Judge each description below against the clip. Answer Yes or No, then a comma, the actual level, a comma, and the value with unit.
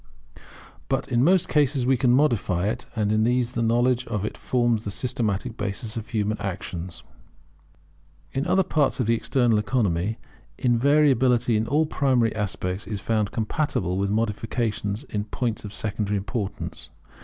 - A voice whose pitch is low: Yes, low, 115 Hz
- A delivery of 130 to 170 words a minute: Yes, average, 155 wpm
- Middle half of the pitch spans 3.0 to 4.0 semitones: Yes, average, 3.4 semitones